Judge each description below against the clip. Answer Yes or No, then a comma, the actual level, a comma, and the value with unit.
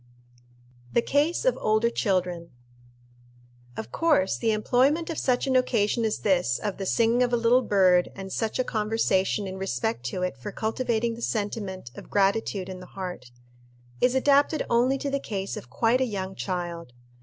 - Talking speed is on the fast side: No, average, 175 wpm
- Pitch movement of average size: Yes, average, 4.6 semitones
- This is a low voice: No, high, 215 Hz